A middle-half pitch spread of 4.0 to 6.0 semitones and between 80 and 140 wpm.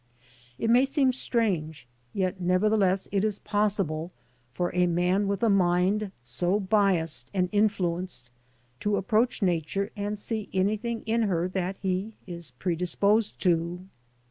No: average, 3.1 semitones; slow, 135 wpm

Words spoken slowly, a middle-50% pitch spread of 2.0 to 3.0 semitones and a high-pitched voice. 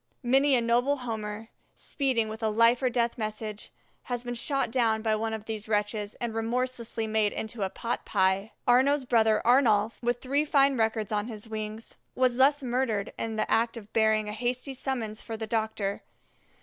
No: average, 185 wpm; narrow, 2.4 semitones; high, 225 Hz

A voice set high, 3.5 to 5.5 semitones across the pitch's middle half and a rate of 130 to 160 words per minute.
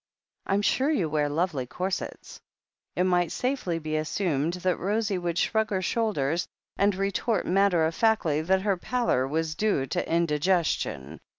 No: medium, 180 Hz; average, 4.3 semitones; average, 155 wpm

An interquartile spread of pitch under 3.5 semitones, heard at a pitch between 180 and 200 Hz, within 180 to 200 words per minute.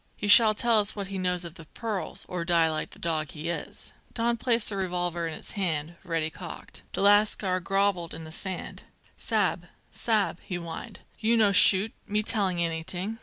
No: average, 3.8 semitones; medium, 185 Hz; average, 190 wpm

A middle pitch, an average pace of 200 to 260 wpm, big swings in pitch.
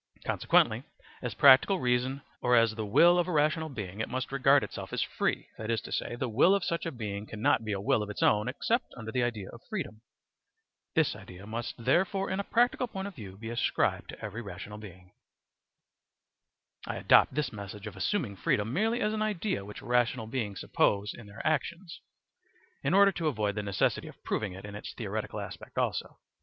No: low, 120 Hz; fast, 205 wpm; wide, 7.5 semitones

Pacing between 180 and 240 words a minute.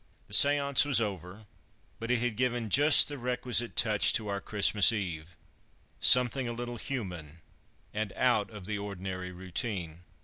No: average, 150 wpm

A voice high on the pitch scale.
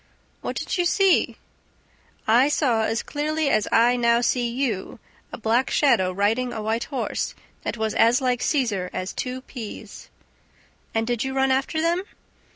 Yes: high, 245 Hz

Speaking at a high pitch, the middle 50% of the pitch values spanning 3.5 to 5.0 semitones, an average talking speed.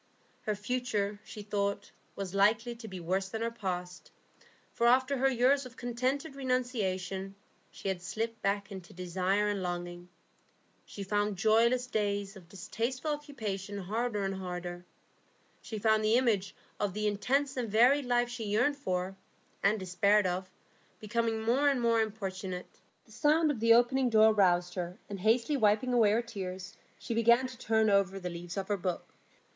Yes: high, 210 Hz; average, 3.9 semitones; average, 165 wpm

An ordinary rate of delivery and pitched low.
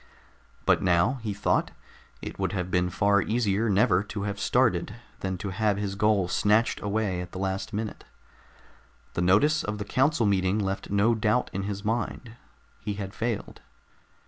Yes: average, 170 wpm; low, 100 Hz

